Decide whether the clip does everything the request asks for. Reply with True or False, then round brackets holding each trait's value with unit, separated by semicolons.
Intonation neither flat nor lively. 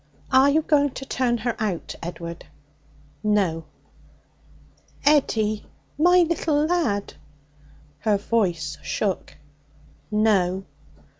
False (7.0 semitones)